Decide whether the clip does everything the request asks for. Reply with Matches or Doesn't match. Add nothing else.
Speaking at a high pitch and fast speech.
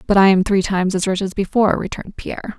Matches